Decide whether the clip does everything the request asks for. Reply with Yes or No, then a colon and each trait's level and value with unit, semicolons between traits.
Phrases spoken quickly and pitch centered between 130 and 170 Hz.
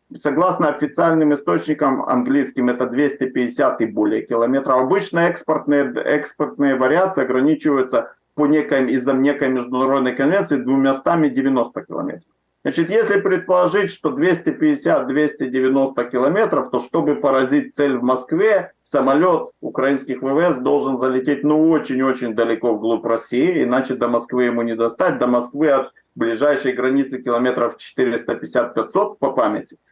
No: average, 120 wpm; low, 135 Hz